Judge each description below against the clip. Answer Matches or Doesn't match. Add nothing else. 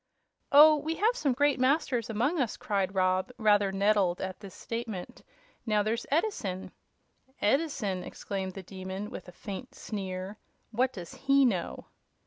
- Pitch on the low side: Doesn't match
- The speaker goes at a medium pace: Matches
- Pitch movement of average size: Doesn't match